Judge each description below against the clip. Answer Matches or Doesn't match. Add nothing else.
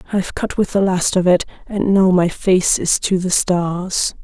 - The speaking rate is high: Matches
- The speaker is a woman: Matches